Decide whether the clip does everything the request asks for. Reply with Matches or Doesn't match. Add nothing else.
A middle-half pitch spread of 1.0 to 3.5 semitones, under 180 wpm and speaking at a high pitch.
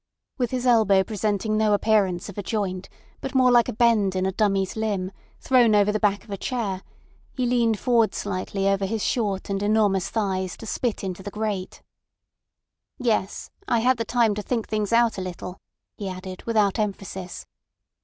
Doesn't match